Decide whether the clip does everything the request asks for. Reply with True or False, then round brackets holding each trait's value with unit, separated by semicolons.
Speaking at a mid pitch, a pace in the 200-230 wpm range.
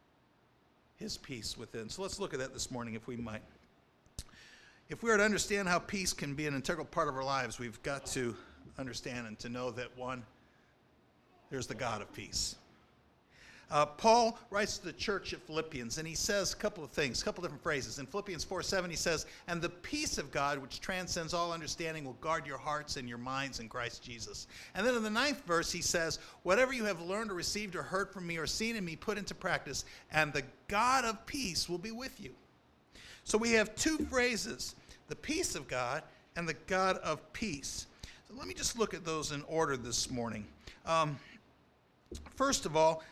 True (160 Hz; 205 wpm)